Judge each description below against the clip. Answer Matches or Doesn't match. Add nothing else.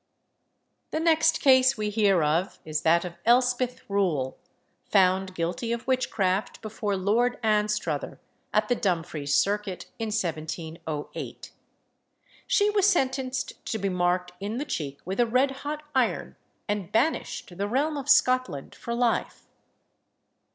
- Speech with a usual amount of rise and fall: Doesn't match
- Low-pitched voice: Doesn't match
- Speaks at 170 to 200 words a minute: Doesn't match